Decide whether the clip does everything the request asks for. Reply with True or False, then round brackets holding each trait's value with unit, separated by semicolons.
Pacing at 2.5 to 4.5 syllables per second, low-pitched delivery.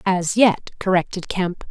False (4.0 syllables/s; 185 Hz)